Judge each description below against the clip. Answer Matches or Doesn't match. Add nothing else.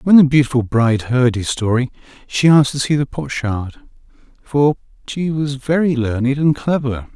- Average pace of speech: Matches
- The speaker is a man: Matches